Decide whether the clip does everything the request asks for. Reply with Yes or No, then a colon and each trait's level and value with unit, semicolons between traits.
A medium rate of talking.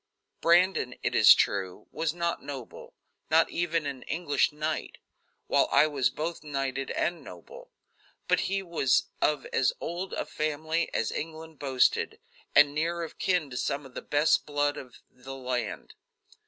Yes: average, 155 wpm